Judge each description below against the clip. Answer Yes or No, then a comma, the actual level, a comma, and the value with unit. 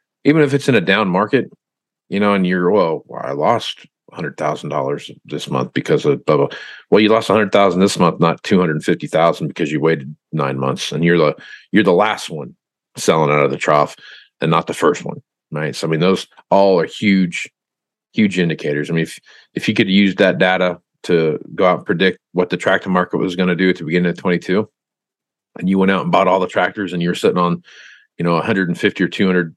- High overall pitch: No, very low, 90 Hz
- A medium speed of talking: No, fast, 235 wpm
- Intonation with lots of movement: No, average, 2.7 semitones